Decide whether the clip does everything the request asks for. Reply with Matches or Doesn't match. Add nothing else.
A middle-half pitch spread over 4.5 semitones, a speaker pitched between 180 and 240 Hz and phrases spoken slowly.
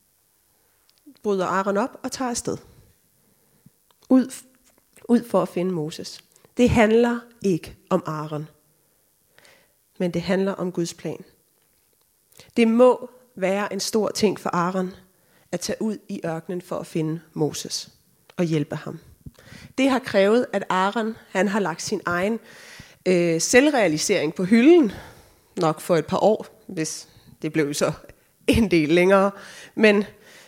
Matches